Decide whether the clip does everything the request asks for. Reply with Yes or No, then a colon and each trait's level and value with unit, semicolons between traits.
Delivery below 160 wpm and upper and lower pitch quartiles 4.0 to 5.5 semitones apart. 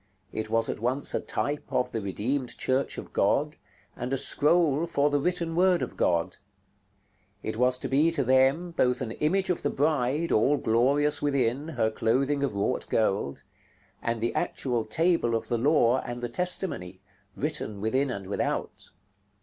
No: average, 170 wpm; average, 4.4 semitones